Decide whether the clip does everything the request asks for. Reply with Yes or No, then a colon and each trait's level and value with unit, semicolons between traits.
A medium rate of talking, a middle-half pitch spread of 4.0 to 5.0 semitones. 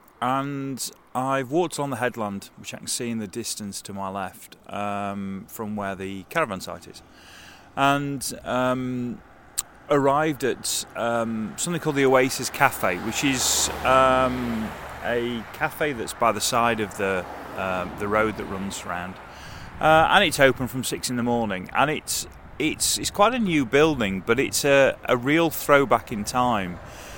Yes: average, 165 wpm; average, 4.7 semitones